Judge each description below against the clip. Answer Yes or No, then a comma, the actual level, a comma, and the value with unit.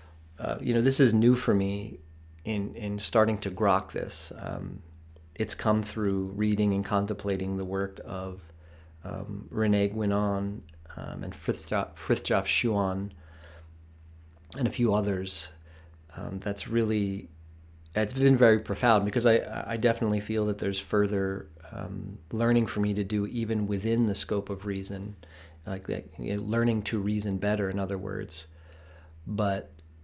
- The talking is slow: No, average, 150 wpm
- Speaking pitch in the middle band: No, low, 100 Hz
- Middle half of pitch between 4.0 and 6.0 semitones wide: Yes, average, 4.3 semitones